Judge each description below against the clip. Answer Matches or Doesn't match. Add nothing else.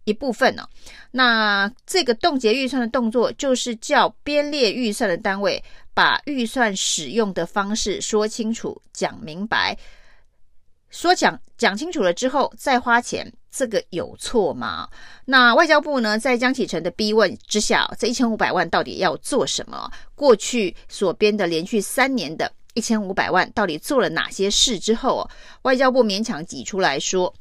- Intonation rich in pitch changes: Doesn't match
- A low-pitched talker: Doesn't match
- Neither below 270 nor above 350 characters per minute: Doesn't match